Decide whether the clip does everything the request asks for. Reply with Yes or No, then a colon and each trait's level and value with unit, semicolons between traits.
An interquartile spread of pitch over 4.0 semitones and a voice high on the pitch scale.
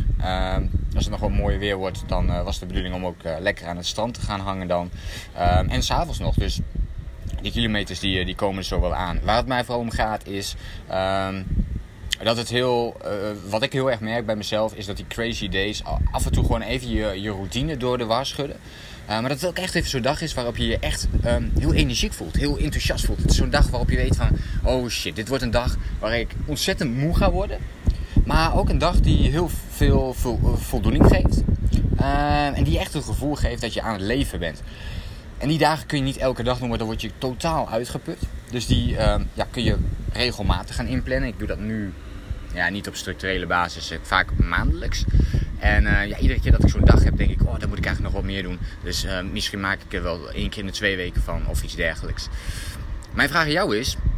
No: average, 4.5 semitones; low, 100 Hz